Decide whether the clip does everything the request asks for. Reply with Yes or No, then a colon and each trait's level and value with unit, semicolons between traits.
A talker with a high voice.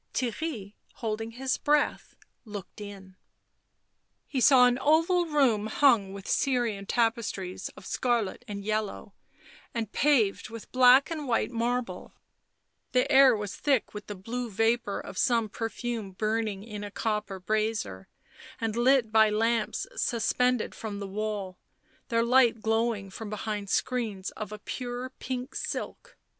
Yes: high, 225 Hz